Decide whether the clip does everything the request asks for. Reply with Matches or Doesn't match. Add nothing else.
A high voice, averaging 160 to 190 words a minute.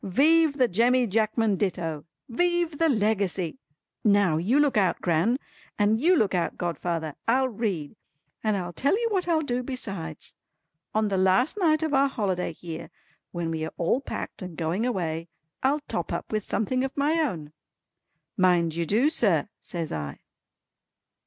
Matches